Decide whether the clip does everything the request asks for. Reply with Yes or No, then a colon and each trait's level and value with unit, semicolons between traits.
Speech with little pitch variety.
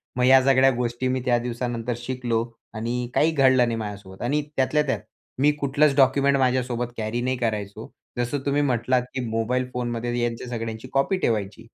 Yes: narrow, 2.3 semitones